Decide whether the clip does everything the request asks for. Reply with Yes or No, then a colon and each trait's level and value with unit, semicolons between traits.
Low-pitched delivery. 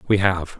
Yes: very low, 95 Hz